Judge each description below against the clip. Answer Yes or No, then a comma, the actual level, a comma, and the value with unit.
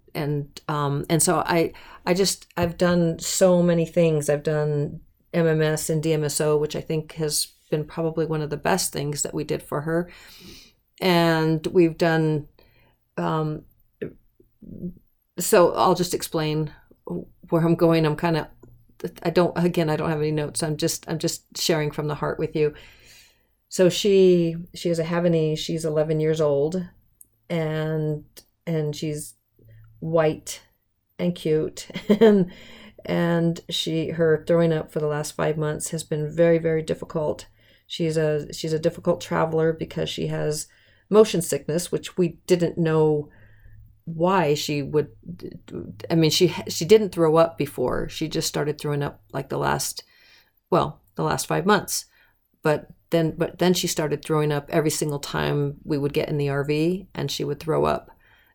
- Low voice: No, medium, 160 Hz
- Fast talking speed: No, average, 160 wpm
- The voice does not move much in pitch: Yes, narrow, 2.2 semitones